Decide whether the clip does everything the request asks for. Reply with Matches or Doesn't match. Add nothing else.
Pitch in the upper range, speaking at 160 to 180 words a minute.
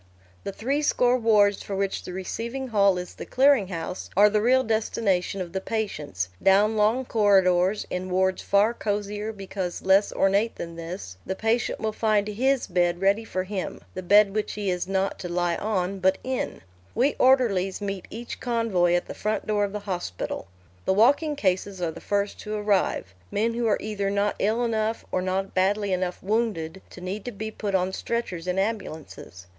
Doesn't match